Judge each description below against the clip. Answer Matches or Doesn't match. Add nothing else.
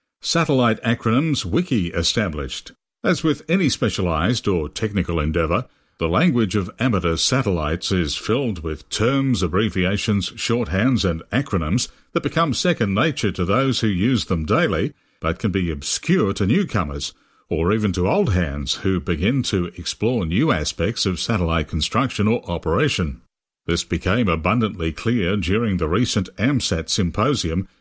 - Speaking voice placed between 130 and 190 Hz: Doesn't match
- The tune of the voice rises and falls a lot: Matches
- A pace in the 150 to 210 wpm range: Doesn't match